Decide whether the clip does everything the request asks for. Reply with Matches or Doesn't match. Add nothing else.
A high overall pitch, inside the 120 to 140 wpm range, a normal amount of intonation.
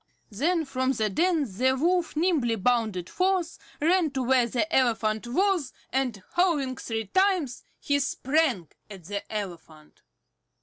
Doesn't match